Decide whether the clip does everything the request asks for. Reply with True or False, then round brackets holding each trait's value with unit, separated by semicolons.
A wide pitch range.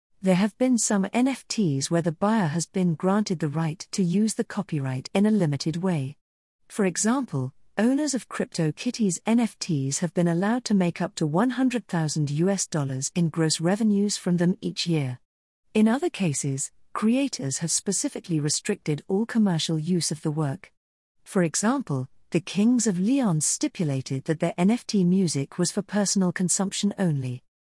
False (4.9 semitones)